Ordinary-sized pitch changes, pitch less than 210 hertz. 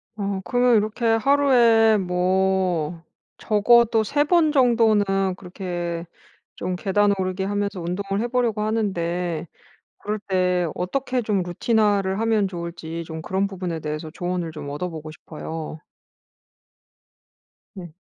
Yes: average, 4.0 semitones; high, 190 Hz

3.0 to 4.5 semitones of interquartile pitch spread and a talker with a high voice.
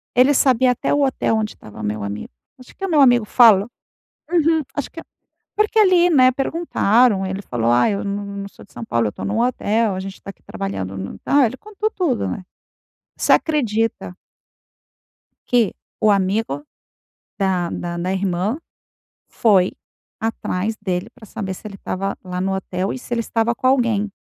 No: average, 5.0 semitones; high, 215 Hz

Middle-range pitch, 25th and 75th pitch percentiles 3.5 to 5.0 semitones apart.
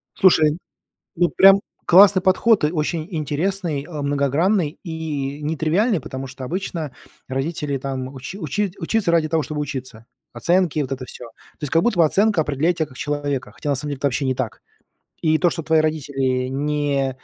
Yes: medium, 150 Hz; average, 3.8 semitones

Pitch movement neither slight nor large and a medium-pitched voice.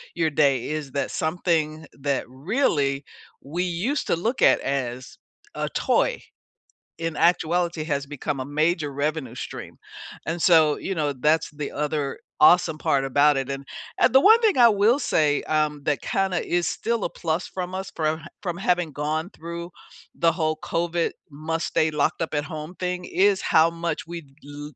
Yes: average, 3.1 semitones; medium, 160 Hz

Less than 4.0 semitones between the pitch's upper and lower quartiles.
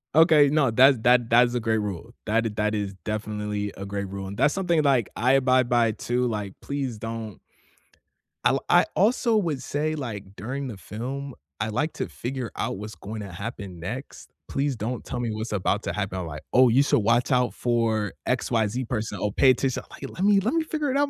No: average, 4.5 semitones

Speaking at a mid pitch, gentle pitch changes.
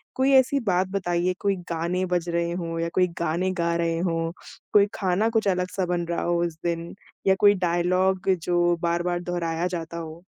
Yes: medium, 175 Hz; narrow, 1.8 semitones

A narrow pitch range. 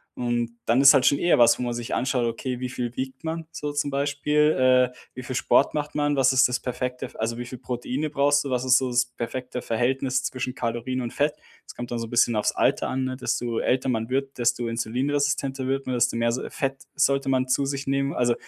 Yes: narrow, 2.2 semitones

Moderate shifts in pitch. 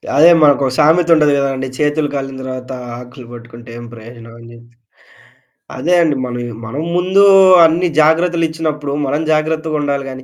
Yes: average, 4.0 semitones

